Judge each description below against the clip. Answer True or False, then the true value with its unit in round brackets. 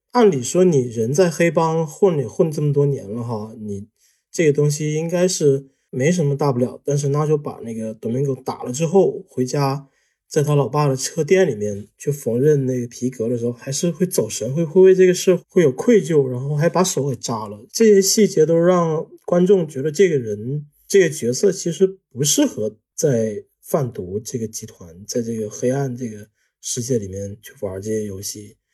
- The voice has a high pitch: False (140 Hz)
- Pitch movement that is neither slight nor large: False (6.4 semitones)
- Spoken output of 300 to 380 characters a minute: False (280 characters per minute)